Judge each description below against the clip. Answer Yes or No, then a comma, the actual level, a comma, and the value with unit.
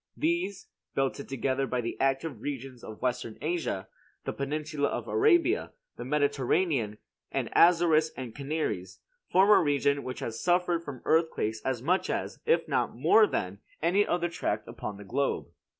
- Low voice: No, medium, 145 Hz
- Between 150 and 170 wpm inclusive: Yes, average, 155 wpm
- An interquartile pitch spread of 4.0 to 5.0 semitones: No, wide, 5.5 semitones